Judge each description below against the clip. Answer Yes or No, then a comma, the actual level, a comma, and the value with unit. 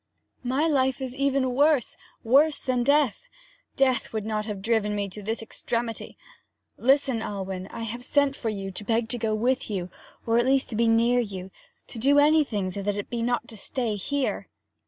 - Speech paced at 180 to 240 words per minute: Yes, average, 195 wpm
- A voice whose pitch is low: No, high, 235 Hz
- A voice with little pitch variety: No, average, 3.9 semitones